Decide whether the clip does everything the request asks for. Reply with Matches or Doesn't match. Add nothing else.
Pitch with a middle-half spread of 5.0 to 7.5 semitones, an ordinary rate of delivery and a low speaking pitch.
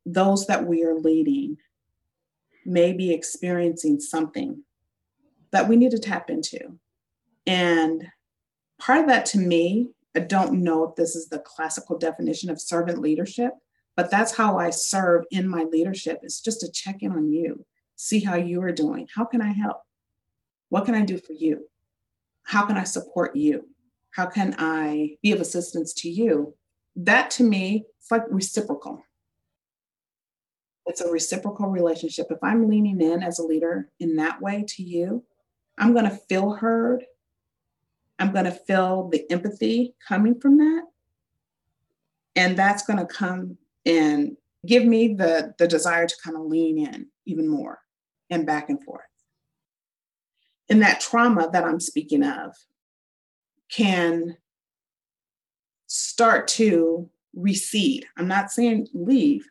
Doesn't match